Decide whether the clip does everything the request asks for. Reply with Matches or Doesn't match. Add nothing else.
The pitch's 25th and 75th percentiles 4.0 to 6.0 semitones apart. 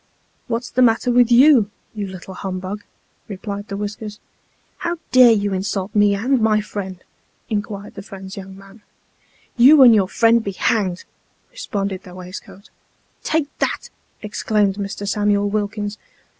Doesn't match